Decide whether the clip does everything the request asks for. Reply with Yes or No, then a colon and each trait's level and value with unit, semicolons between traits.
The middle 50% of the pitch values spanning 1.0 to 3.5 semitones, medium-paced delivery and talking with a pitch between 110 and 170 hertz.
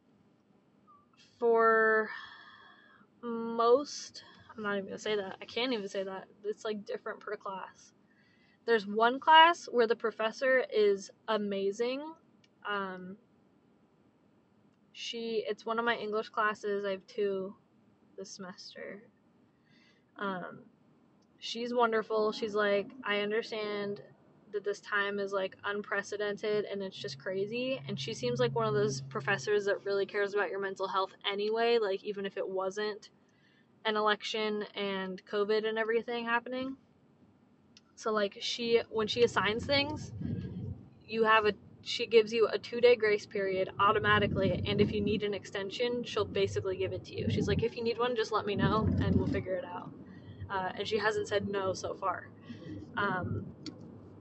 No: narrow, 2.5 semitones; average, 155 wpm; high, 210 Hz